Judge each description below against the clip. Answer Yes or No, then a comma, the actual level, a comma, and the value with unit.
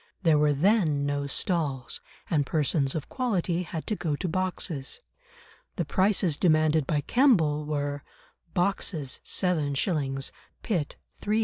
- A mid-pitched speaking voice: Yes, medium, 155 Hz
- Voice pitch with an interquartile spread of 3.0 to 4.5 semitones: Yes, average, 4.2 semitones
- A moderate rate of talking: No, slow, 125 wpm